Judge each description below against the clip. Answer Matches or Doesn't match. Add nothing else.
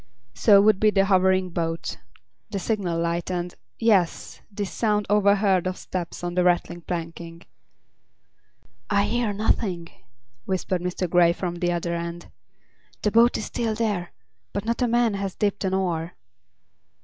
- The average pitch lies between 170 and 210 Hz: Matches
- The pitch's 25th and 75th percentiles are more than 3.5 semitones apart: Doesn't match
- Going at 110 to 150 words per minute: Matches